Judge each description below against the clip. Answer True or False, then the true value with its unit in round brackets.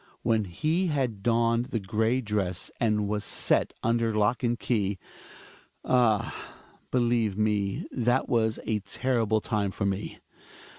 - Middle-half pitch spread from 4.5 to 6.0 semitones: False (2.5 semitones)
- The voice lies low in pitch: True (110 Hz)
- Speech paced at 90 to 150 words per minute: True (140 wpm)